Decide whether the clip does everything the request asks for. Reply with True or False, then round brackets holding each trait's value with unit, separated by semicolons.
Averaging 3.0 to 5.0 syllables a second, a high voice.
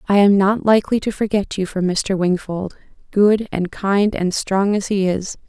True (4.5 syllables/s; 195 Hz)